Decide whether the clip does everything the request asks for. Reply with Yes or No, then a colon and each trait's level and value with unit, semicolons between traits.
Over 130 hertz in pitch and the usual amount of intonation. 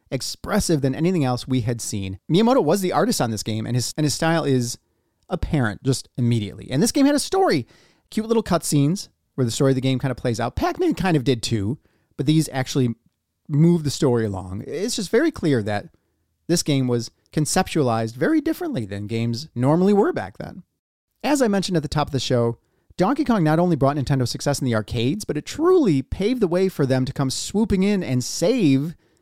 No: medium, 140 Hz; wide, 7.4 semitones